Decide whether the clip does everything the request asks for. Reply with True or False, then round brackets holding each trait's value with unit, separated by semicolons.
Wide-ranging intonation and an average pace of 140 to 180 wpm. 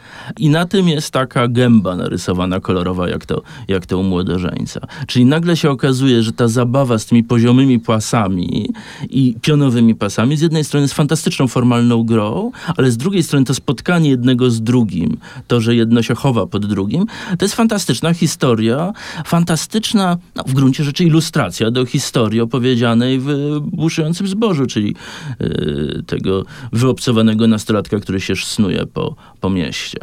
True (5.8 semitones; 155 wpm)